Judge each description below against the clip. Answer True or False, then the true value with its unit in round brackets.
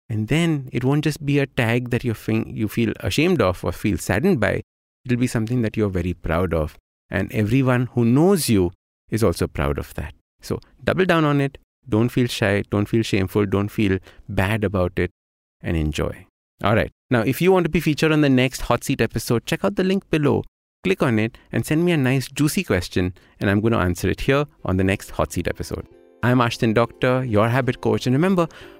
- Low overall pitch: True (115 Hz)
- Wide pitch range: True (5.8 semitones)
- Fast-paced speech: True (220 wpm)